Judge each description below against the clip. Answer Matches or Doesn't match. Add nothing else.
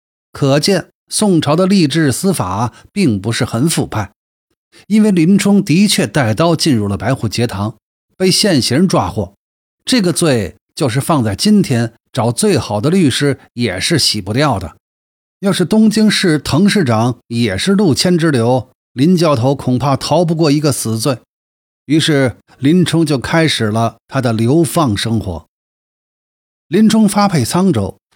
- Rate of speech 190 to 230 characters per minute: Matches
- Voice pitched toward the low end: Doesn't match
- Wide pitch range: Matches